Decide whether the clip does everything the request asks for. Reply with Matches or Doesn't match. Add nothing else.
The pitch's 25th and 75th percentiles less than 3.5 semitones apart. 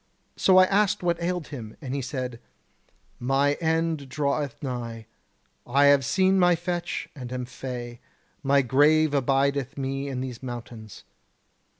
Doesn't match